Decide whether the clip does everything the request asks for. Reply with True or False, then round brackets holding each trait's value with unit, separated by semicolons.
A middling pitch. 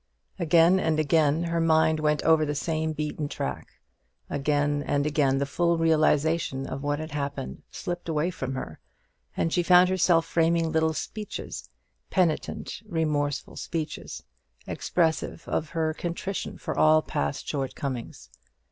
True (155 Hz)